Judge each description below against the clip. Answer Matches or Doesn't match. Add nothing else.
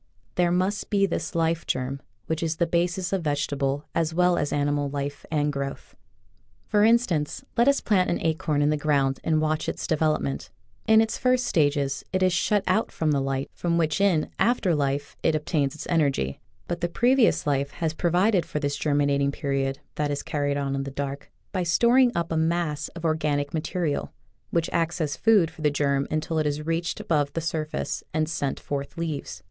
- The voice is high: Doesn't match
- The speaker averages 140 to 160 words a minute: Doesn't match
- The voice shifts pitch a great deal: Doesn't match